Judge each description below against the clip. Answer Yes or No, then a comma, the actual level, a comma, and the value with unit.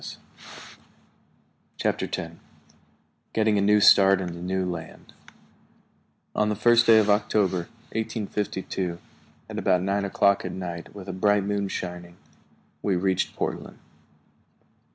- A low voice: Yes, low, 100 Hz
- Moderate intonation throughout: No, narrow, 2.3 semitones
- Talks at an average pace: No, slow, 130 wpm